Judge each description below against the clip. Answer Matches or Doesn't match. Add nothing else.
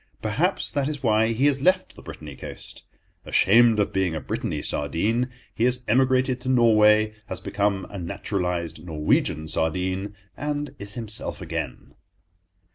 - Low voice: Matches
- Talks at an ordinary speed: Matches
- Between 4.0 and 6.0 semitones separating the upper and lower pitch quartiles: Matches